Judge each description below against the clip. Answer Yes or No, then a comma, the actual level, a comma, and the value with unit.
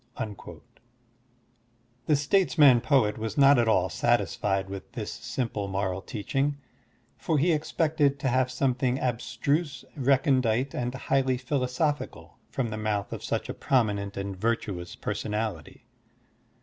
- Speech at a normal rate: No, slow, 130 wpm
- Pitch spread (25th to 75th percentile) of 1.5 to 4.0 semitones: No, average, 4.9 semitones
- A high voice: No, low, 125 Hz